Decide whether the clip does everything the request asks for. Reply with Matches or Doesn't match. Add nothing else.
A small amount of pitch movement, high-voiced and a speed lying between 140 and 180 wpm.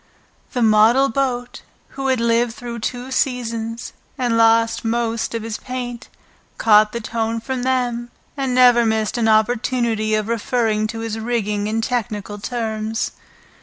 Matches